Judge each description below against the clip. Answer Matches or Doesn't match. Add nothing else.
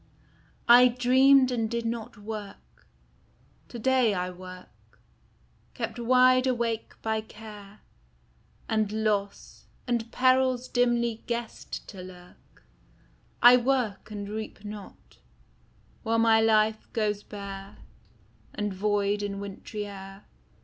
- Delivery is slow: Matches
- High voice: Matches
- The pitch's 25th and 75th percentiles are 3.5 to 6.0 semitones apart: Doesn't match